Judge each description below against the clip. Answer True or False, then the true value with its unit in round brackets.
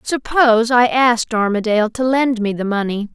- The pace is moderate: True (170 wpm)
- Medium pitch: False (230 Hz)